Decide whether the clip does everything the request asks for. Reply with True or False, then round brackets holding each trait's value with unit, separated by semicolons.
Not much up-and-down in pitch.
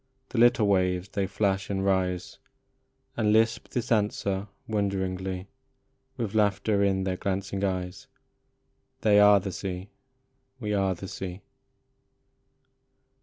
True (1.7 semitones)